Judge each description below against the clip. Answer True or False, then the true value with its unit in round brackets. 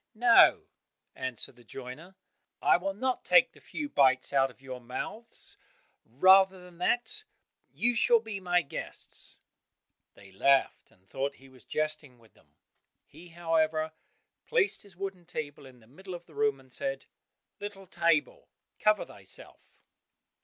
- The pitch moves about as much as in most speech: False (6.7 semitones)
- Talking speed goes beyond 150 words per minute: False (145 wpm)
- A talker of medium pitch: True (165 Hz)